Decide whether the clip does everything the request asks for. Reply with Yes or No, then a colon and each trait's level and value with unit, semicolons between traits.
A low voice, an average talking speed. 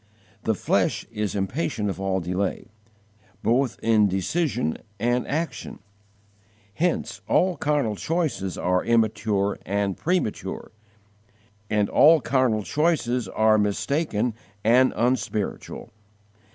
No: low, 115 Hz; slow, 100 wpm